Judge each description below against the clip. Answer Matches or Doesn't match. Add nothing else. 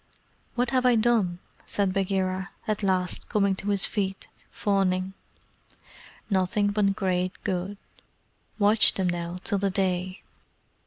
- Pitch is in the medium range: Doesn't match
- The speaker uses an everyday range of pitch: Doesn't match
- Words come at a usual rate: Doesn't match